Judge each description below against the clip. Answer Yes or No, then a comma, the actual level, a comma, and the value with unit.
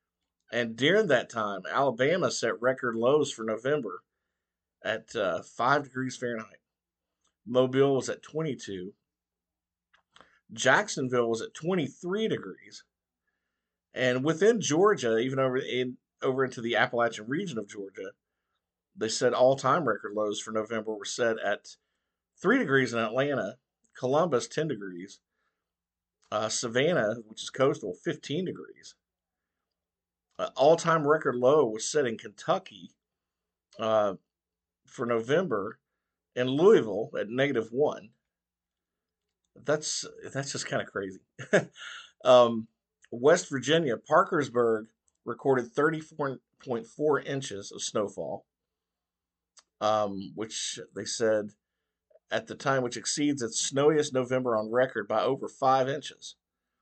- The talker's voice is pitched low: Yes, low, 125 Hz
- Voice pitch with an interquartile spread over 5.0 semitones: No, average, 4.0 semitones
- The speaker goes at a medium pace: No, slow, 120 wpm